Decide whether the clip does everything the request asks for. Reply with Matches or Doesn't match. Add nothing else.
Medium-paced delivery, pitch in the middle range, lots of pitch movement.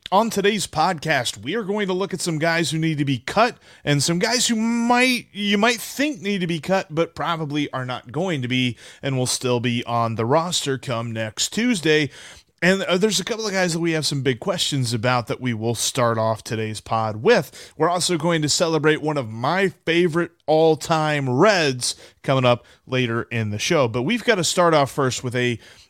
Doesn't match